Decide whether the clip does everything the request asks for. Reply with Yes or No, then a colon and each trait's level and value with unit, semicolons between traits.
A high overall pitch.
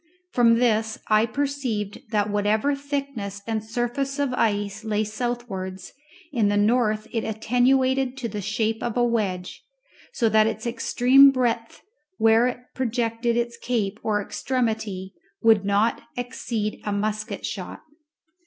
Yes: high, 225 Hz